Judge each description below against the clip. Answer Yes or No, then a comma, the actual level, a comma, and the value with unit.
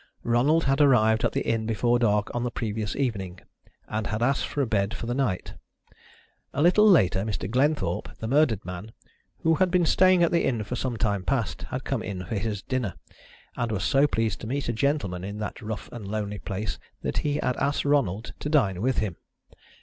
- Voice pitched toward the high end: No, low, 115 Hz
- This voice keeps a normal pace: No, fast, 210 wpm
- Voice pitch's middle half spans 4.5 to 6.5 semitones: Yes, average, 5.0 semitones